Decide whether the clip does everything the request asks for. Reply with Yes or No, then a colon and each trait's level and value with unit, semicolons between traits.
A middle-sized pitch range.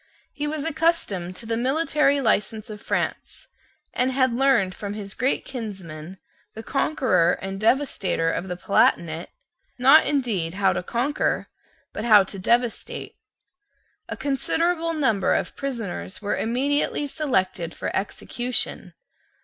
No: wide, 6.2 semitones